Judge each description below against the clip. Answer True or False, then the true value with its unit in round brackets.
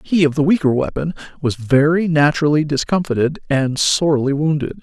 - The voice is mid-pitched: True (150 Hz)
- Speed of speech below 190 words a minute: True (150 wpm)